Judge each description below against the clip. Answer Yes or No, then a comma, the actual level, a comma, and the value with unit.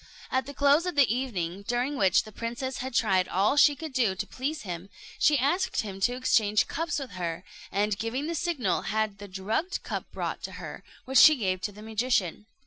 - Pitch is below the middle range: No, high, 230 Hz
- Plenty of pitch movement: Yes, wide, 5.7 semitones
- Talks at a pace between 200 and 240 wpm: Yes, fast, 205 wpm